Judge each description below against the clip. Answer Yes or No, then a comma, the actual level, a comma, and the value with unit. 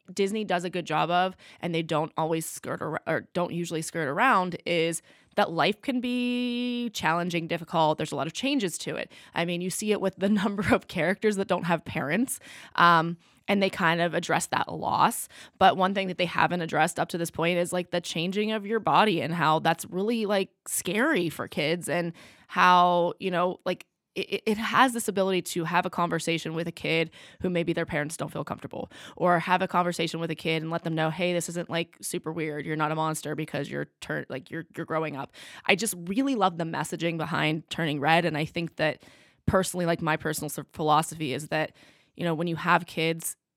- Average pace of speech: No, fast, 215 wpm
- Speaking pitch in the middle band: Yes, medium, 170 Hz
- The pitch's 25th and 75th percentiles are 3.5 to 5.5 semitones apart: No, narrow, 2.5 semitones